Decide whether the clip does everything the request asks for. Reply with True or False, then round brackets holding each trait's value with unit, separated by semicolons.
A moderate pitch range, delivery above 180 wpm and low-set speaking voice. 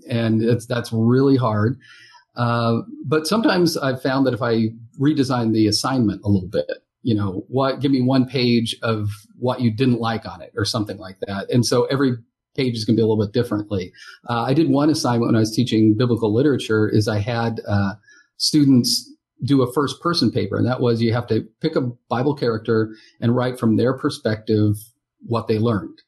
True (3.2 semitones; 200 wpm; 120 Hz)